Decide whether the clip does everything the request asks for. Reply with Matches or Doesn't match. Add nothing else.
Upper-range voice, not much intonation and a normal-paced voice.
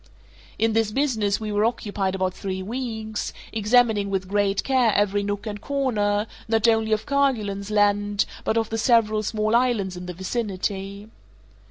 Matches